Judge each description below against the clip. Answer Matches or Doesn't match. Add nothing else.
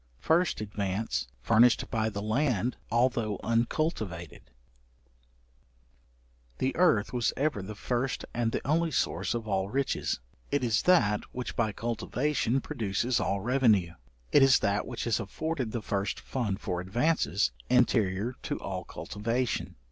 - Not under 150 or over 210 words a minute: Doesn't match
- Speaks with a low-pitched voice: Matches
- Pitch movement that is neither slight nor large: Matches